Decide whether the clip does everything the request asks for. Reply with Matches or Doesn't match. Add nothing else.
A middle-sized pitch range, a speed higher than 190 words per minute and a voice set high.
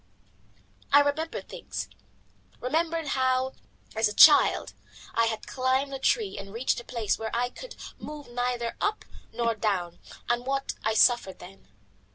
Doesn't match